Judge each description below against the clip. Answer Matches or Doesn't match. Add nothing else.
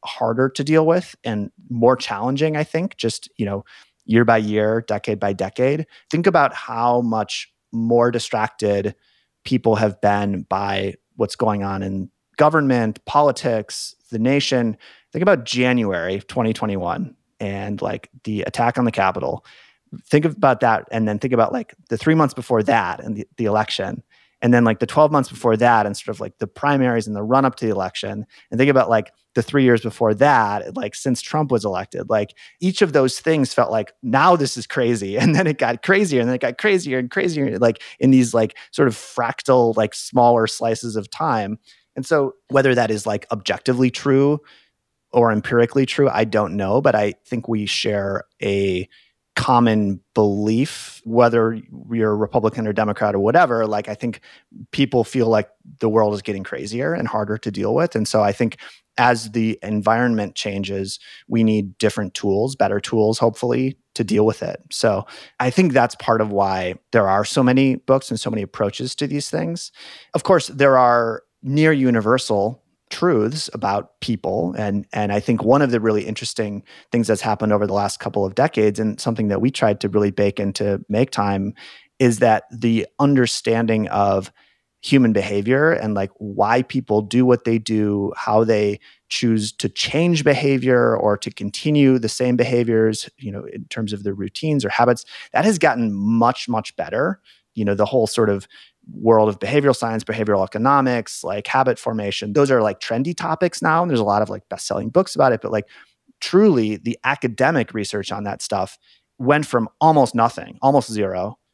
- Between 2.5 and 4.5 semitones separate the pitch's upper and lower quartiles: Matches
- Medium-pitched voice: Doesn't match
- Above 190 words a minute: Doesn't match